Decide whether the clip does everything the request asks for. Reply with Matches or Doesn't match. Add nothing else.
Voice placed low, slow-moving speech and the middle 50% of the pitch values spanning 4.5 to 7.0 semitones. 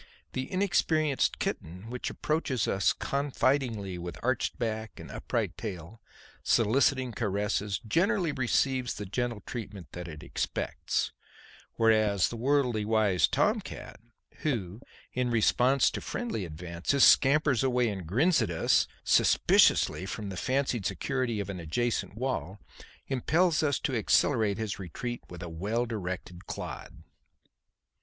Matches